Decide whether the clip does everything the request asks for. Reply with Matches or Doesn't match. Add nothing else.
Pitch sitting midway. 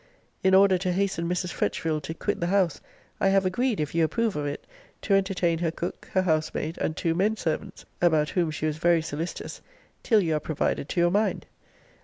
Matches